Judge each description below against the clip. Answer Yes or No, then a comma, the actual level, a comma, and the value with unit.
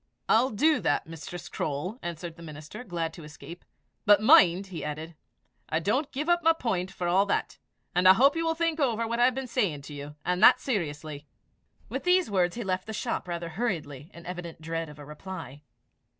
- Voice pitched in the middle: Yes, medium, 180 Hz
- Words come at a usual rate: No, fast, 210 wpm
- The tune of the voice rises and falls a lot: Yes, wide, 6.5 semitones